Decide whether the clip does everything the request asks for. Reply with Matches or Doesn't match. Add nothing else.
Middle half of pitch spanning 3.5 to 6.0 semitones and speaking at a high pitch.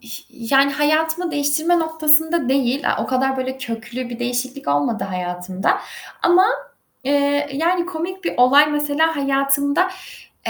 Matches